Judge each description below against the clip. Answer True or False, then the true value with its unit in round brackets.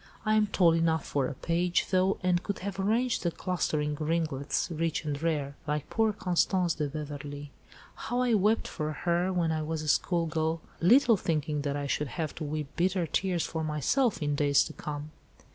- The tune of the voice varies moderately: True (3.6 semitones)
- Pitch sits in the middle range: True (165 Hz)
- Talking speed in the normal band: True (195 wpm)